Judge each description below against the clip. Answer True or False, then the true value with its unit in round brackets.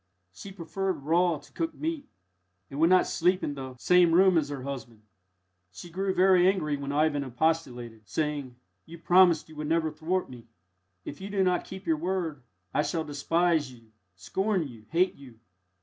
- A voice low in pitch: False (160 Hz)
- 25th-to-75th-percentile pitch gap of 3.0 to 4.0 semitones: False (4.5 semitones)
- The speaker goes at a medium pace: True (180 wpm)